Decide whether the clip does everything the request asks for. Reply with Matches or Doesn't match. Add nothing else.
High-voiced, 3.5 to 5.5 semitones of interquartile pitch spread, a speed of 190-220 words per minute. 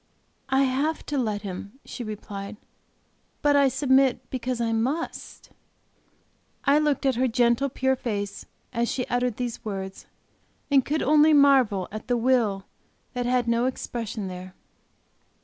Doesn't match